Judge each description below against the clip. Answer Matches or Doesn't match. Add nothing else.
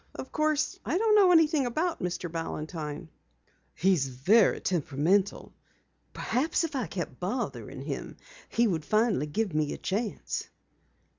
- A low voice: Doesn't match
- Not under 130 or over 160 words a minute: Matches